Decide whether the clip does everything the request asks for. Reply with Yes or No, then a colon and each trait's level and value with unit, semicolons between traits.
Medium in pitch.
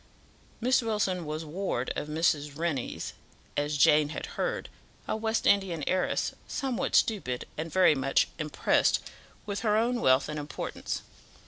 Yes: medium, 165 Hz